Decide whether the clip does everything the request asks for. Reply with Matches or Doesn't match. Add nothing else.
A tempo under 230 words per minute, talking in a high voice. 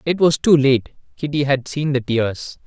Doesn't match